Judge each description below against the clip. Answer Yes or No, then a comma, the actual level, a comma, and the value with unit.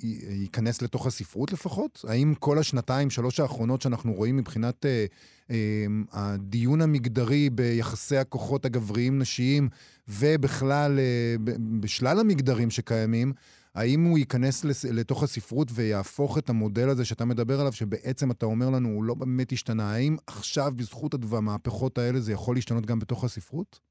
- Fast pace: No, average, 140 wpm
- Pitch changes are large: No, average, 3.1 semitones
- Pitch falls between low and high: No, low, 125 Hz